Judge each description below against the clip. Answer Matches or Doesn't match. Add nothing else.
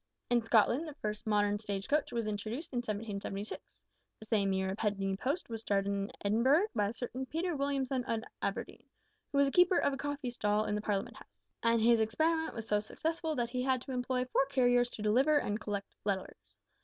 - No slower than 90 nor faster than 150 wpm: Doesn't match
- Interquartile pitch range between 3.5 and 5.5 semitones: Matches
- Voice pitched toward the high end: Matches